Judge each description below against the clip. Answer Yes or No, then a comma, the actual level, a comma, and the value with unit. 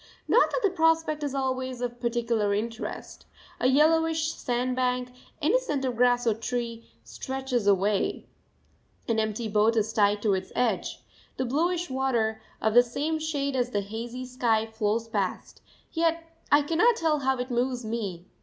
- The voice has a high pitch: Yes, high, 245 Hz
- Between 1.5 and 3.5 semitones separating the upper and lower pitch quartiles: No, average, 4.4 semitones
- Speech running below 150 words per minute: No, average, 155 wpm